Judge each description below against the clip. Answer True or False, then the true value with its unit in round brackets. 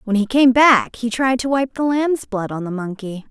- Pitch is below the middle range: False (235 Hz)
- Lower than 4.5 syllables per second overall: False (4.8 syllables/s)